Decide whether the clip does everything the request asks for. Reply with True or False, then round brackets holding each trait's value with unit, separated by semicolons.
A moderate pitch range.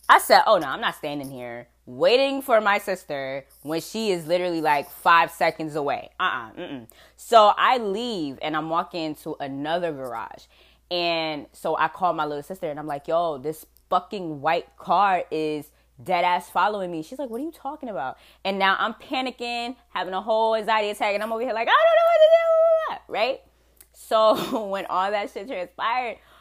False (6.0 semitones)